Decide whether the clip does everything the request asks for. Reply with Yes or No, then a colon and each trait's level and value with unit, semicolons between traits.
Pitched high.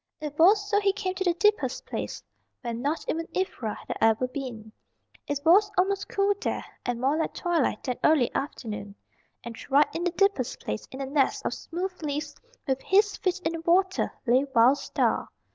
Yes: very high, 315 Hz